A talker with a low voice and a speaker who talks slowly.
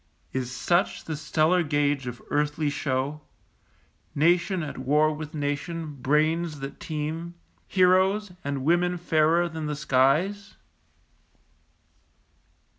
No: medium, 155 Hz; slow, 110 wpm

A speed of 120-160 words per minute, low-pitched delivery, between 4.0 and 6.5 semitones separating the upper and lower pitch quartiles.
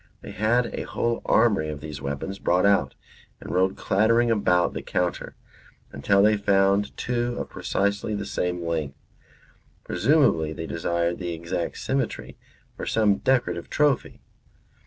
Yes: average, 140 wpm; low, 100 Hz; average, 4.5 semitones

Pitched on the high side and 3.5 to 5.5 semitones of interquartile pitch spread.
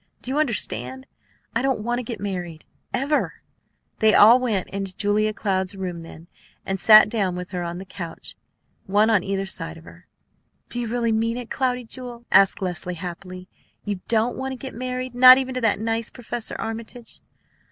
Yes: high, 215 Hz; average, 4.7 semitones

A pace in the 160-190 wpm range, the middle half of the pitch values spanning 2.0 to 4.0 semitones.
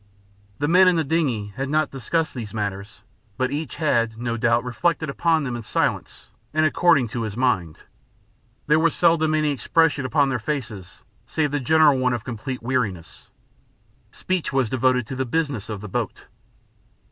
No: average, 170 wpm; average, 5.2 semitones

